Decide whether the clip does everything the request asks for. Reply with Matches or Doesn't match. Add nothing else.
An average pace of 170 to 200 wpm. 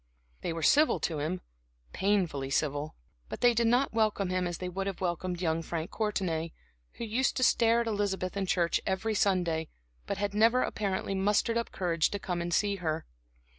Matches